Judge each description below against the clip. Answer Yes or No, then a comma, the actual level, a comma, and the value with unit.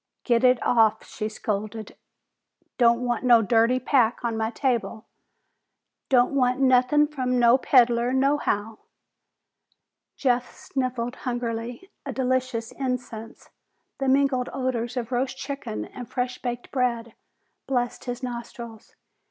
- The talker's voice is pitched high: Yes, high, 245 Hz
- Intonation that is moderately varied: No, narrow, 1.8 semitones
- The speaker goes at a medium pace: No, slow, 120 wpm